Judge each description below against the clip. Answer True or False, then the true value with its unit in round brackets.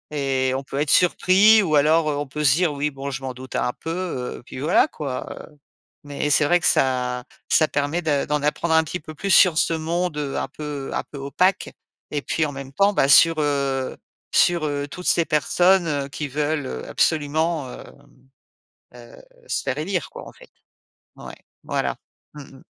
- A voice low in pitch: False (150 Hz)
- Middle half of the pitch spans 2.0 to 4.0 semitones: True (3.2 semitones)